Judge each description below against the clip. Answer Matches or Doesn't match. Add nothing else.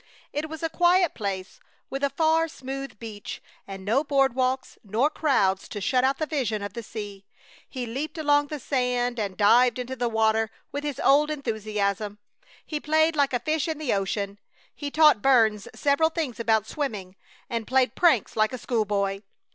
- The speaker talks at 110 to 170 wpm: Doesn't match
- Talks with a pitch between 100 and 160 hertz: Doesn't match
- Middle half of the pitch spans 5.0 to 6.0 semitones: Matches